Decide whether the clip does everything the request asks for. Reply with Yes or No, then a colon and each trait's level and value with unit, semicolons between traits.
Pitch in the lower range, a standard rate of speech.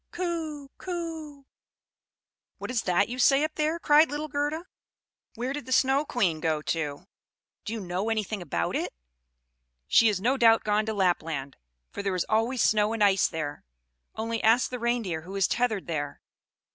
No: high, 225 Hz; average, 170 wpm